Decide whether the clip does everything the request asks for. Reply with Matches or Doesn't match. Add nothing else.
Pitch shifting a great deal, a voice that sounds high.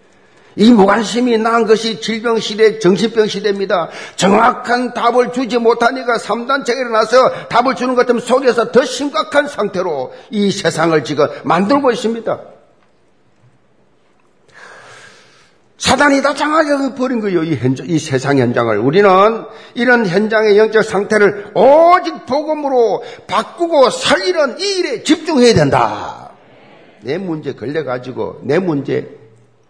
Doesn't match